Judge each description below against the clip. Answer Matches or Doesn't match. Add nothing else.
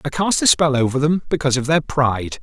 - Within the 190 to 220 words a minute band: Doesn't match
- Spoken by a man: Matches